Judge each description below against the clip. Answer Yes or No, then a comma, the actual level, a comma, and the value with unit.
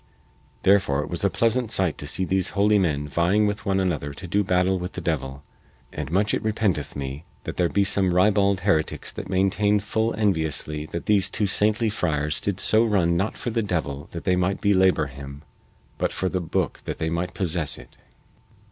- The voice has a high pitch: No, very low, 95 Hz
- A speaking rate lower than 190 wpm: No, average, 200 wpm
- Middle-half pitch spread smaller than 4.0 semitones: No, average, 4.4 semitones